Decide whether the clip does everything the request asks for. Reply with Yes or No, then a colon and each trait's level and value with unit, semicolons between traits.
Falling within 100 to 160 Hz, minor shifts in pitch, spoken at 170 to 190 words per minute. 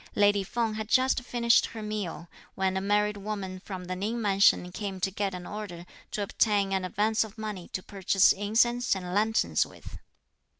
No: high, 205 Hz; narrow, 2.2 semitones; average, 180 wpm